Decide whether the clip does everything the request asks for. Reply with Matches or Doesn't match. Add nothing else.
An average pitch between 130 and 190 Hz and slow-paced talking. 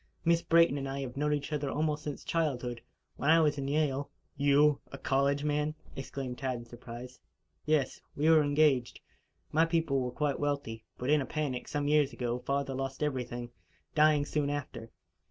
Doesn't match